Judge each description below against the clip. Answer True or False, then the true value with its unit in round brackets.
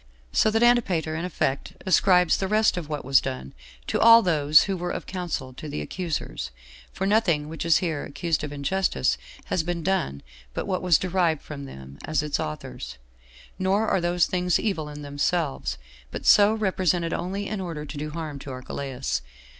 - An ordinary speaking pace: True (185 wpm)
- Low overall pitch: False (165 Hz)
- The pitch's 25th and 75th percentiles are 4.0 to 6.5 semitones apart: True (4.7 semitones)